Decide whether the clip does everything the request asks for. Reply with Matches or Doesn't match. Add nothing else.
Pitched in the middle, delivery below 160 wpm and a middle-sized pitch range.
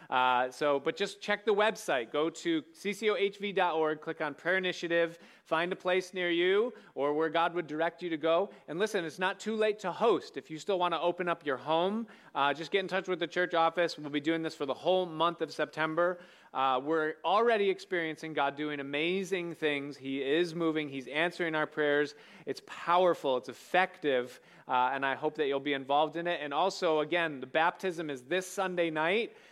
Doesn't match